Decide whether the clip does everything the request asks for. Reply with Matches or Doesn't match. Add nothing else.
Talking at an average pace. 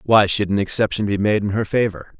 Doesn't match